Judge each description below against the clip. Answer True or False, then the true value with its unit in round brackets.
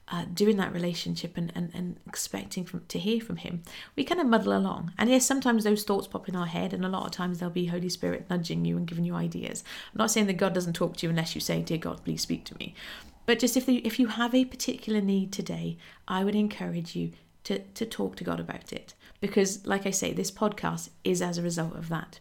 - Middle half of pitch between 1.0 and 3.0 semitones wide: False (3.7 semitones)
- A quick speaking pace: True (255 wpm)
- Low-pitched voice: False (185 Hz)